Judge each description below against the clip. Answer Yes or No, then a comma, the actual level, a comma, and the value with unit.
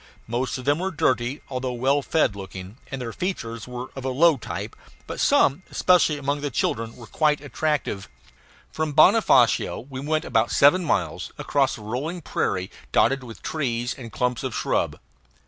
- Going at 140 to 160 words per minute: No, average, 170 wpm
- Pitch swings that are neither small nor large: Yes, average, 4.2 semitones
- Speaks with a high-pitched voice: No, low, 130 Hz